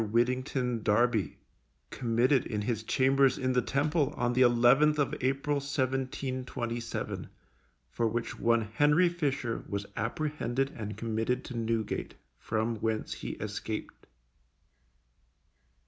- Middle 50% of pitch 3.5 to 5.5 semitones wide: No, average, 2.9 semitones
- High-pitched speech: No, low, 125 Hz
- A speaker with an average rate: No, slow, 115 wpm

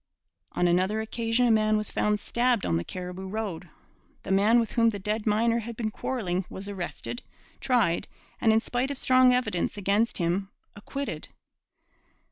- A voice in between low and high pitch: No, high, 215 Hz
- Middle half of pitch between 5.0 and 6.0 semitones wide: No, average, 3.6 semitones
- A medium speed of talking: Yes, average, 165 wpm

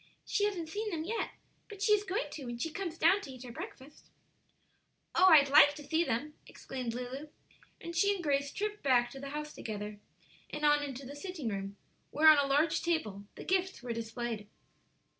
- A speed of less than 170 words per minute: No, average, 200 wpm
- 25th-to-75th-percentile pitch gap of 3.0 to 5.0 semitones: No, wide, 5.5 semitones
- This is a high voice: Yes, very high, 295 Hz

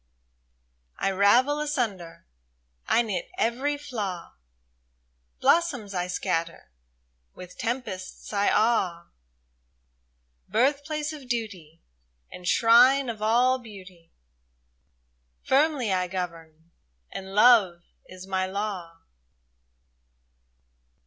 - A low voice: No, high, 200 Hz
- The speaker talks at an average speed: No, slow, 90 wpm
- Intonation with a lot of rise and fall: Yes, wide, 5.7 semitones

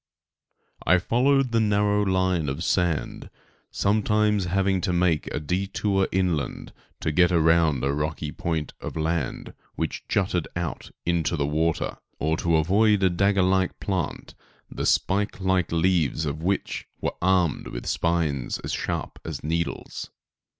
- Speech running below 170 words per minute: Yes, average, 145 wpm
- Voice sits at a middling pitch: No, very low, 90 Hz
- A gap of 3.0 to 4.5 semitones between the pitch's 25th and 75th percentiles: Yes, average, 3.4 semitones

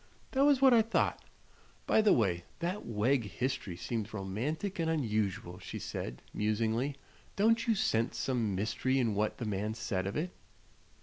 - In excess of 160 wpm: Yes, average, 170 wpm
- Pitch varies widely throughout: Yes, wide, 7.7 semitones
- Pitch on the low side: Yes, low, 115 Hz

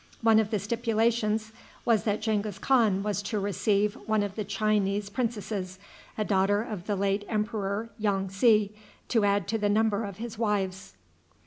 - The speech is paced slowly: No, average, 165 wpm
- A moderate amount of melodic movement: No, narrow, 1.7 semitones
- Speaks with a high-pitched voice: Yes, high, 210 Hz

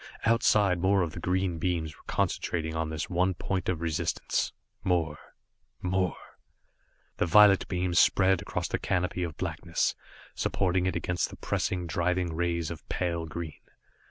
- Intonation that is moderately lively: No, narrow, 1.9 semitones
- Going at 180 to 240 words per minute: No, average, 150 wpm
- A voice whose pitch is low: Yes, very low, 90 Hz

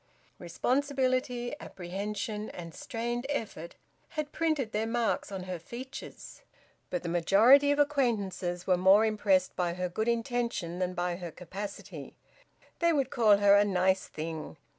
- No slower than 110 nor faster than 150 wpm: Yes, average, 140 wpm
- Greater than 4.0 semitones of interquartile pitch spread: Yes, average, 5.1 semitones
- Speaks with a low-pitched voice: No, high, 205 Hz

